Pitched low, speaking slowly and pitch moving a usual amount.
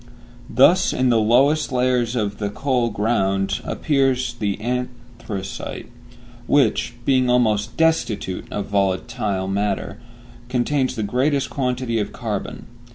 Yes: low, 120 Hz; slow, 115 wpm; average, 3.8 semitones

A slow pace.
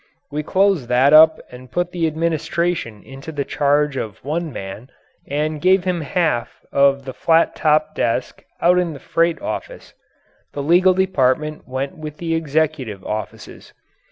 No: average, 155 wpm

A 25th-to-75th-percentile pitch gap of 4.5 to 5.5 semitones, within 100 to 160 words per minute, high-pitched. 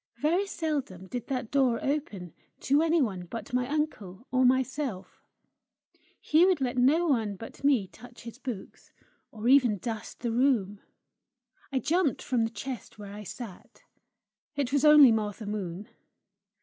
Yes: average, 4.9 semitones; average, 150 wpm; high, 245 Hz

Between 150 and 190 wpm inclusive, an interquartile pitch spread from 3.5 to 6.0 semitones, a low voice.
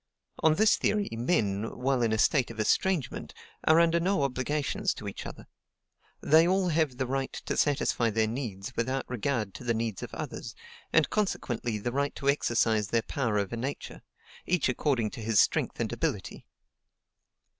Yes: average, 170 wpm; average, 5.2 semitones; low, 130 Hz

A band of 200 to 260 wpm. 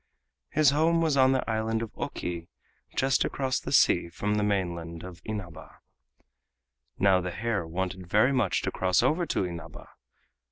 No: average, 165 wpm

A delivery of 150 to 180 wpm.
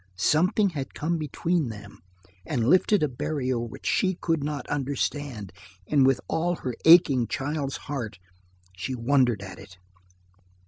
No: average, 140 wpm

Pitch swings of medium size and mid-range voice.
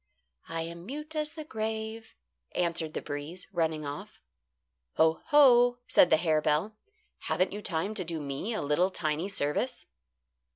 No: wide, 5.8 semitones; medium, 175 Hz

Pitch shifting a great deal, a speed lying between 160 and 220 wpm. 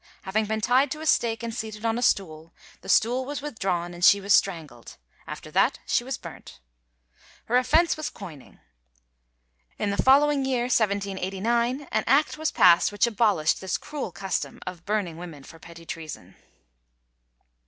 Yes: wide, 5.8 semitones; average, 165 wpm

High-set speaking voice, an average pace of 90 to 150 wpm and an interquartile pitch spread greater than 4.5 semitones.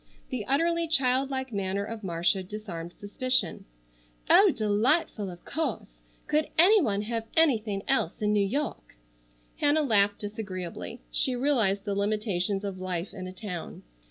Yes: high, 210 Hz; average, 145 wpm; average, 5.2 semitones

